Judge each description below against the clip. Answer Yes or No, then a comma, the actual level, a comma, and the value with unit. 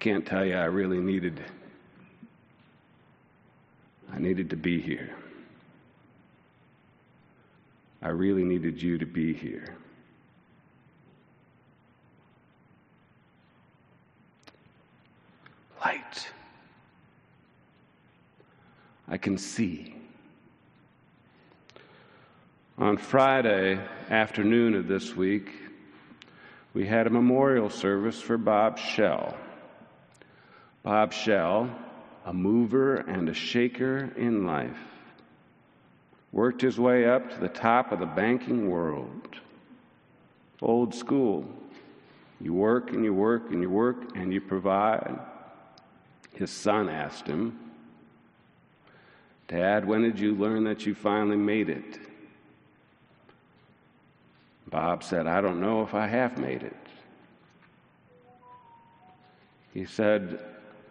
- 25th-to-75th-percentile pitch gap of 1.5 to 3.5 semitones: No, average, 3.9 semitones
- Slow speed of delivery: Yes, slow, 95 wpm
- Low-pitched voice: Yes, low, 105 Hz